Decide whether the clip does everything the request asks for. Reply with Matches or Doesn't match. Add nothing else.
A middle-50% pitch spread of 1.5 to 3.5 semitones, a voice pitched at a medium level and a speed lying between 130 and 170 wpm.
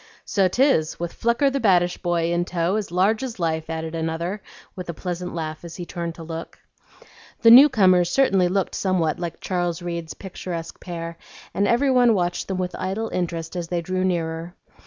Doesn't match